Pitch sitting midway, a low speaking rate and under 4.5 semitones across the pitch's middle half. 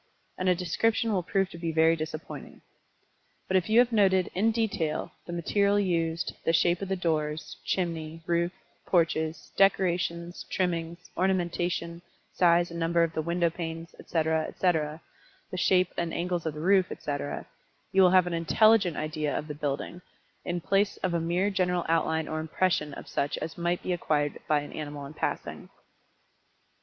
No: medium, 170 Hz; average, 170 wpm; narrow, 2.4 semitones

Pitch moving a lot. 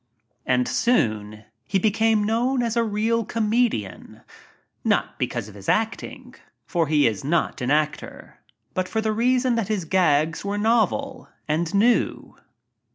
Yes: wide, 7.1 semitones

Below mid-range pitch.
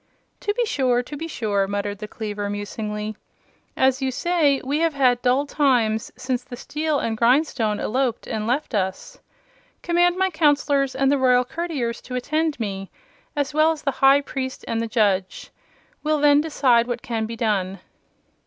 No: very high, 255 Hz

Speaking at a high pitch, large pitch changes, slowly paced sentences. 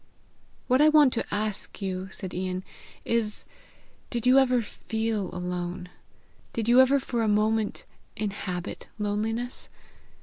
No: high, 215 Hz; average, 4.2 semitones; slow, 130 wpm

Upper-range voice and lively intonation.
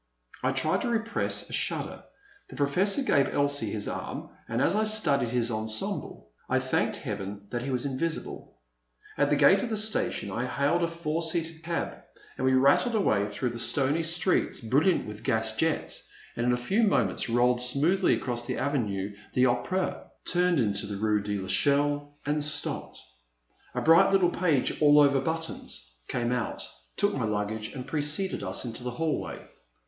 No: low, 135 Hz; wide, 6.4 semitones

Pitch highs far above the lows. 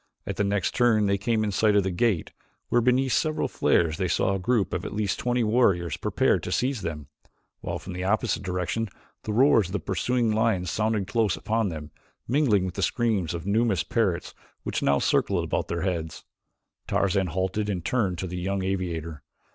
No: average, 3.8 semitones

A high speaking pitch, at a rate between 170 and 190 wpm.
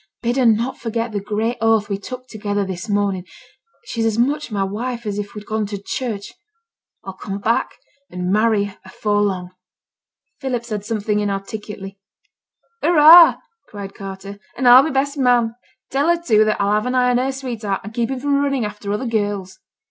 Yes: high, 215 Hz; average, 185 wpm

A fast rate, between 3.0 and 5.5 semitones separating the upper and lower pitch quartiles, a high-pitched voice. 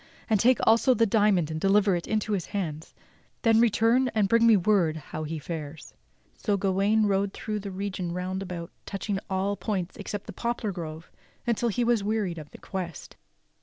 No: average, 190 wpm; average, 3.7 semitones; high, 195 Hz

